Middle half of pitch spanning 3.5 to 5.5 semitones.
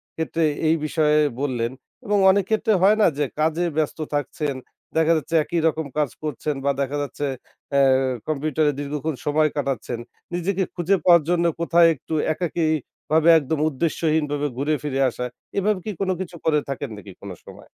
No: average, 2.9 semitones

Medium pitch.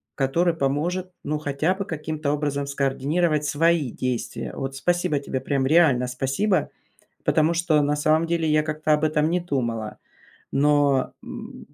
Yes: medium, 150 Hz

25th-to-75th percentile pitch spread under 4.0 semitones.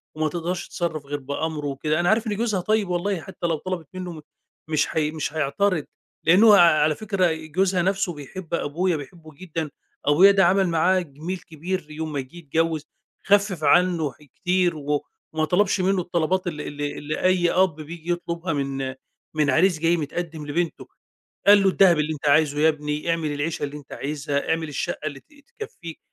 Yes: average, 3.5 semitones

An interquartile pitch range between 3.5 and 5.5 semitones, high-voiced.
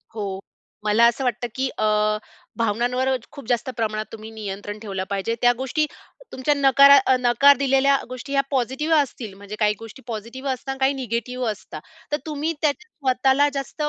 Yes: average, 3.8 semitones; very high, 255 Hz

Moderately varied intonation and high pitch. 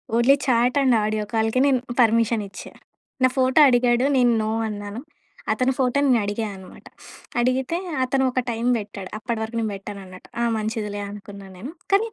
Yes: average, 3.4 semitones; high, 230 Hz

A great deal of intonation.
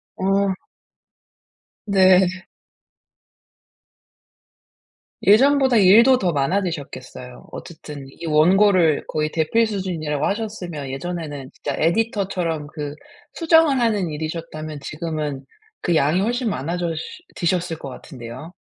No: average, 4.8 semitones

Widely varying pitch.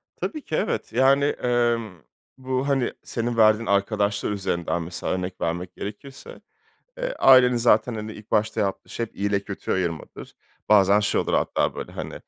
No: average, 3.8 semitones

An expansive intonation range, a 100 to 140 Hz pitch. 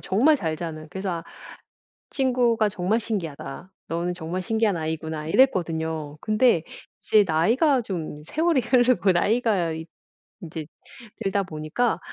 No: wide, 6.1 semitones; medium, 185 Hz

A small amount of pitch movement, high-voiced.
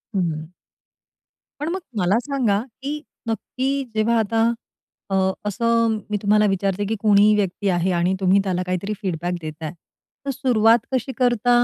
No: average, 4.1 semitones; high, 210 Hz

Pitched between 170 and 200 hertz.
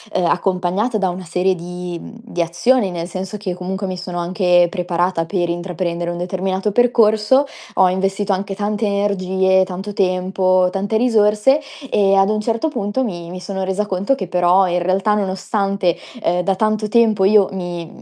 Yes: high, 190 Hz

